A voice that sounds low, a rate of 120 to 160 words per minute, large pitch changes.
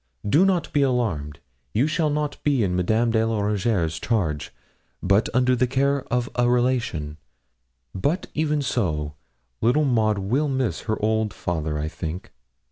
Yes: low, 115 Hz; average, 155 wpm; wide, 6.5 semitones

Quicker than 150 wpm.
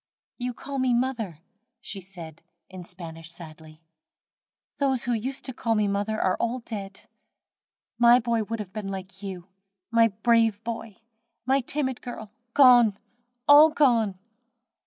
No: average, 140 wpm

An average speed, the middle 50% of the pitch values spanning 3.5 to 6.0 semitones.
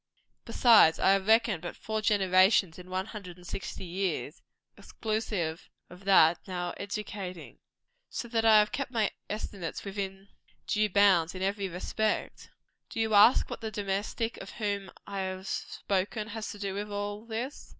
No: average, 160 wpm; narrow, 2.4 semitones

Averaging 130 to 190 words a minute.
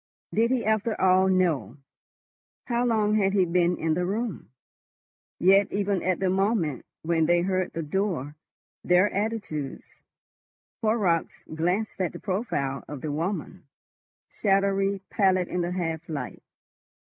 Yes: slow, 135 wpm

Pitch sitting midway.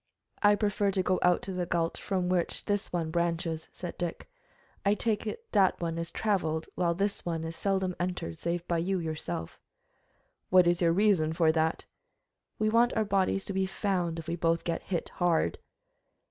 Yes: medium, 175 Hz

